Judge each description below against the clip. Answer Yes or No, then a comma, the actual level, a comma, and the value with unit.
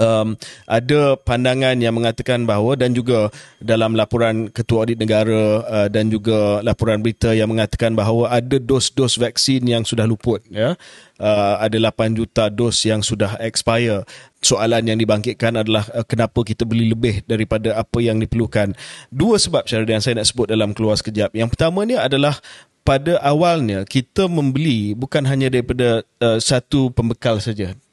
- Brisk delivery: Yes, fast, 160 wpm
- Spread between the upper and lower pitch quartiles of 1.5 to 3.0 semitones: Yes, narrow, 2.4 semitones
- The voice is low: Yes, low, 115 Hz